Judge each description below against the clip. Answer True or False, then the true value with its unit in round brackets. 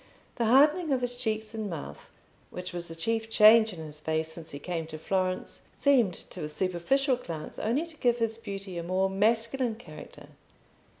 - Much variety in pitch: True (5.7 semitones)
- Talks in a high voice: True (205 Hz)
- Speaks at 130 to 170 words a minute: False (185 wpm)